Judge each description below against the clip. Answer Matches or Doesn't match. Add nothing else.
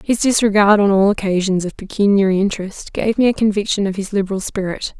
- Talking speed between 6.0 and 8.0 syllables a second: Matches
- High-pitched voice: Matches